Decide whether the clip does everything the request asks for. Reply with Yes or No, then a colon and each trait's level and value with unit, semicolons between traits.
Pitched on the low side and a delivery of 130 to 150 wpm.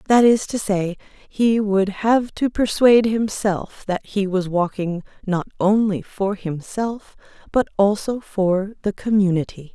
No: high, 205 Hz; average, 140 wpm